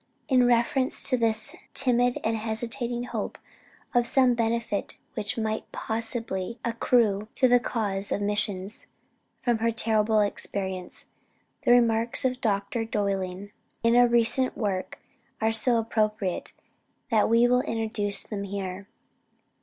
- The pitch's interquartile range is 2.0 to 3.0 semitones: Yes, average, 2.7 semitones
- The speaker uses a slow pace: Yes, slow, 130 wpm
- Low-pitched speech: No, high, 225 Hz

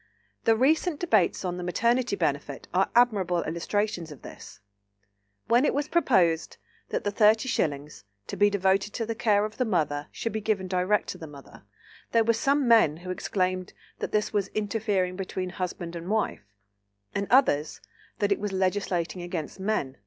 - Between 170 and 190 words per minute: Yes, average, 175 wpm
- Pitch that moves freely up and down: No, average, 3.8 semitones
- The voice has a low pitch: No, high, 195 Hz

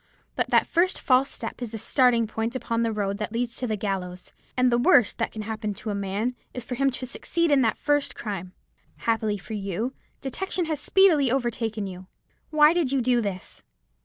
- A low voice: No, high, 230 Hz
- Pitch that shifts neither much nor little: Yes, average, 3.9 semitones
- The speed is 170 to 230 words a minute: Yes, fast, 205 wpm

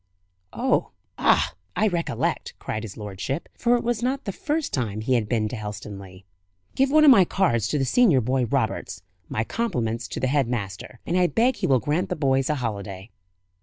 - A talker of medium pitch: No, low, 130 Hz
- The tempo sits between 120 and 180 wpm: No, average, 200 wpm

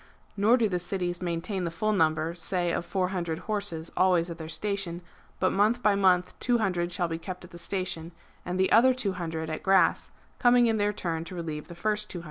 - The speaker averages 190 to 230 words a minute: Yes, fast, 205 wpm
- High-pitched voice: No, medium, 180 Hz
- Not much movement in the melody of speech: No, average, 3.3 semitones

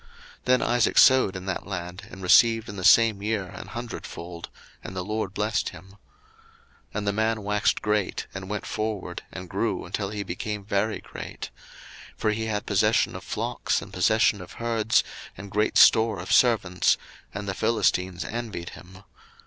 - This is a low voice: Yes, low, 105 Hz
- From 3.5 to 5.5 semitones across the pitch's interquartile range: No, average, 2.9 semitones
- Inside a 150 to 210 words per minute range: Yes, average, 175 wpm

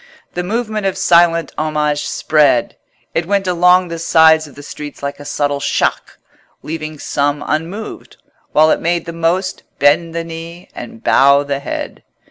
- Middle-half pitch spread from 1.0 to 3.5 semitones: Yes, average, 3.0 semitones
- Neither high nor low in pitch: Yes, medium, 165 Hz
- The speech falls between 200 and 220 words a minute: No, average, 160 wpm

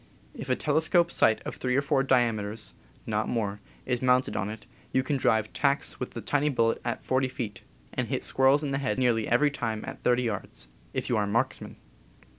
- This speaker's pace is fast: Yes, fast, 225 wpm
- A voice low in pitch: Yes, low, 125 Hz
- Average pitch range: Yes, average, 3.5 semitones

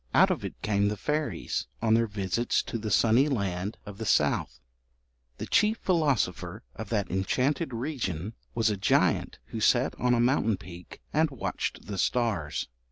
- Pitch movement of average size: Yes, average, 4.6 semitones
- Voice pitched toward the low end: Yes, low, 110 Hz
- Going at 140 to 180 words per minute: Yes, average, 165 wpm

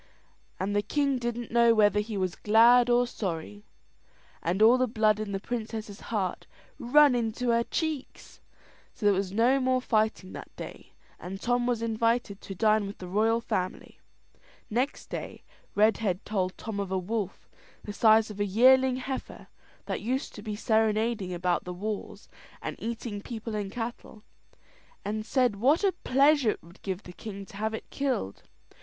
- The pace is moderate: Yes, average, 170 wpm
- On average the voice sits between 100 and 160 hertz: No, high, 220 Hz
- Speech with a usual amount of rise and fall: Yes, average, 3.2 semitones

